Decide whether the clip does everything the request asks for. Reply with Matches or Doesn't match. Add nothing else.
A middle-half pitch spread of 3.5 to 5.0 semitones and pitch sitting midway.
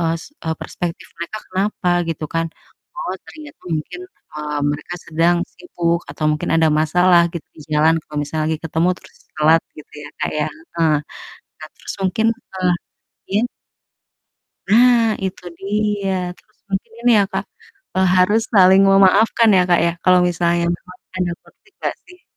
Matches